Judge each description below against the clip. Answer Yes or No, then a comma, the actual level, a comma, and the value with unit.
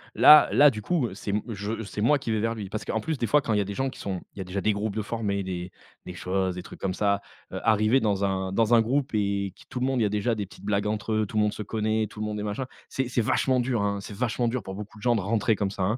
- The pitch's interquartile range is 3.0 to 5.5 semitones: No, narrow, 2.5 semitones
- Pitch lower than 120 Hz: Yes, low, 105 Hz